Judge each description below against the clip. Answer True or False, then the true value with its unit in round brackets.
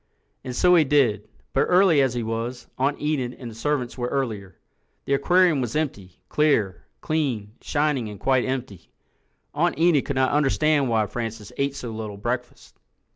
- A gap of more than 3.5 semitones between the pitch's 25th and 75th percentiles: True (4.6 semitones)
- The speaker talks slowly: False (160 wpm)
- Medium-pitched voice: False (130 Hz)